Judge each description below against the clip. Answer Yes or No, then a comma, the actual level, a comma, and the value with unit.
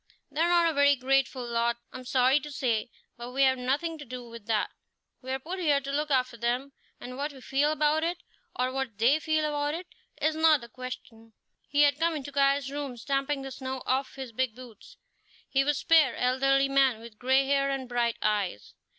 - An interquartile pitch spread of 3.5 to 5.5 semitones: No, narrow, 2.6 semitones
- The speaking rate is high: Yes, fast, 210 wpm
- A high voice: Yes, very high, 270 Hz